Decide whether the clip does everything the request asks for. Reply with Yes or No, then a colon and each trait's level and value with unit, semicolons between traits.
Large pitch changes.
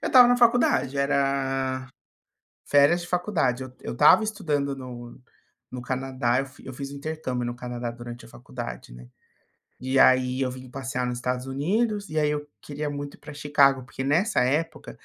No: average, 2.9 semitones